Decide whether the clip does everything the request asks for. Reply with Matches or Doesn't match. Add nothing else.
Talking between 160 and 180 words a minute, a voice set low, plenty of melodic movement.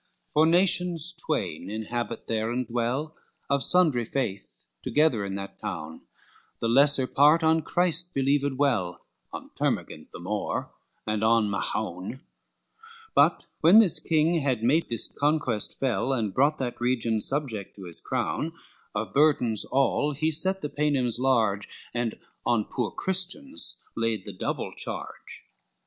Doesn't match